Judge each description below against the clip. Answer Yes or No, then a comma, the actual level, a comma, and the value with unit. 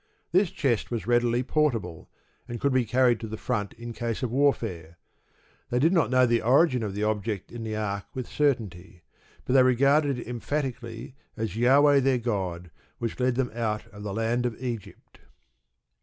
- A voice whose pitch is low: Yes, low, 120 Hz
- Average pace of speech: Yes, average, 180 wpm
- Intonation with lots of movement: No, average, 3.2 semitones